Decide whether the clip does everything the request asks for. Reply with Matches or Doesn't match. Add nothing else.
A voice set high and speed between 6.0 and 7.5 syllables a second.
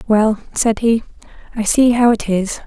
Doesn't match